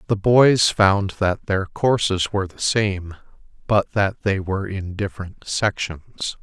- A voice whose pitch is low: Yes, low, 100 Hz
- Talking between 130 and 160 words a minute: Yes, average, 150 wpm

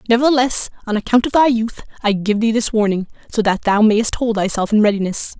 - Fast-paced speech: Yes, fast, 210 wpm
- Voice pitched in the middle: No, high, 220 Hz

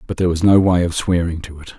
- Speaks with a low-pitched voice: Yes, very low, 85 Hz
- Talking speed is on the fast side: Yes, fast, 305 wpm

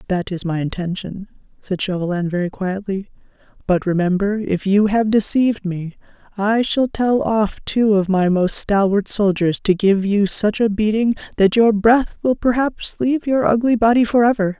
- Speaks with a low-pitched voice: No, high, 205 Hz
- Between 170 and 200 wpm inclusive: Yes, average, 175 wpm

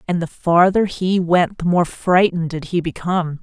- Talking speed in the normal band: Yes, average, 195 wpm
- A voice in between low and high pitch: Yes, medium, 175 Hz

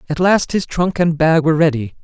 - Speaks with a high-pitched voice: No, medium, 160 Hz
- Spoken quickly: Yes, fast, 235 wpm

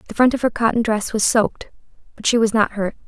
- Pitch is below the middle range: No, high, 220 Hz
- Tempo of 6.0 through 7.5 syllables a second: Yes, 6.4 syllables/s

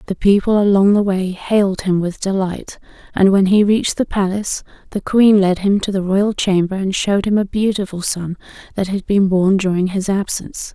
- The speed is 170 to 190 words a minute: No, average, 200 wpm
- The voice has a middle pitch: No, high, 195 Hz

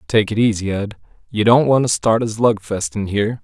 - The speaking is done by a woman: No, male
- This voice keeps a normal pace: No, fast, 225 wpm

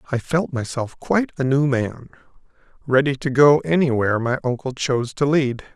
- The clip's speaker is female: No, male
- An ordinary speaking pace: Yes, average, 165 wpm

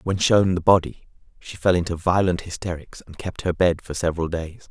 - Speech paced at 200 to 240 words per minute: Yes, fast, 205 wpm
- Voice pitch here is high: No, very low, 90 Hz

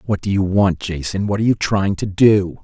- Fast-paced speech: Yes, fast, 230 wpm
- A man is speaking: Yes, male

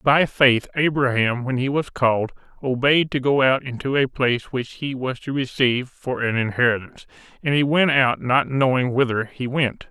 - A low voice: Yes, low, 130 Hz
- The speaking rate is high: No, average, 190 wpm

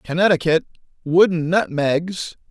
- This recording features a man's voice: Yes, male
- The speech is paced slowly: Yes, slow, 70 wpm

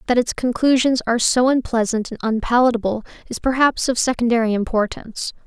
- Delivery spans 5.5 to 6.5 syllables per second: Yes, 5.9 syllables/s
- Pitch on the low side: No, high, 240 Hz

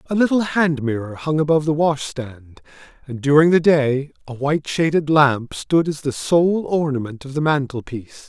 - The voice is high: No, medium, 145 Hz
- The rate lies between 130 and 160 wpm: No, average, 175 wpm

